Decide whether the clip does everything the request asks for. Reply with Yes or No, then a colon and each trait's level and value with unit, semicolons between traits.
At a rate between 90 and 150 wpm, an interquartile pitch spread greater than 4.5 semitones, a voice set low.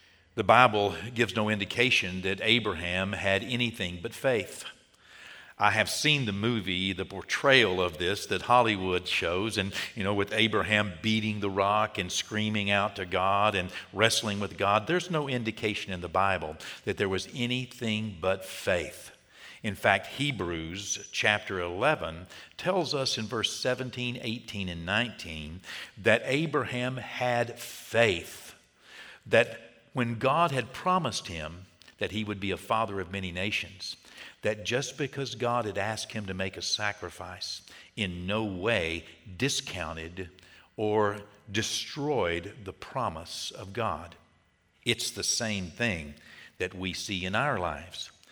No: average, 145 wpm; average, 3.8 semitones; low, 105 Hz